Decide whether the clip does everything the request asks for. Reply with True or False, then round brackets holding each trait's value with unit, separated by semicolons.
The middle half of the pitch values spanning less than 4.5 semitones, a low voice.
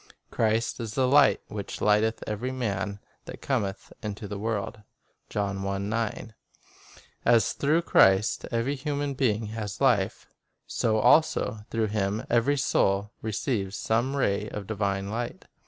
True (3.1 semitones; 110 Hz)